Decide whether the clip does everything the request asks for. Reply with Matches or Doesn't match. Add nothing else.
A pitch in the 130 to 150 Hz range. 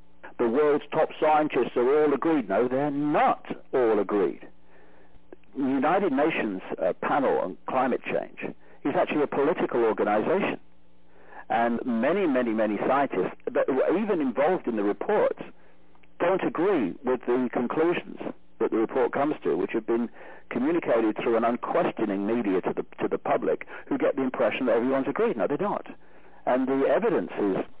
Doesn't match